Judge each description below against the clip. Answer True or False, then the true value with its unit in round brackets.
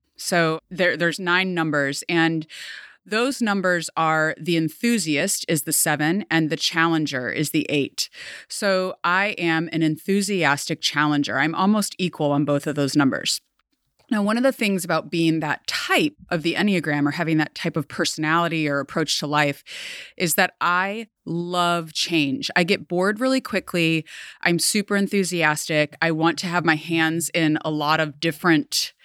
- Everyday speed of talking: True (165 wpm)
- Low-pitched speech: False (165 Hz)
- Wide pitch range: False (3.3 semitones)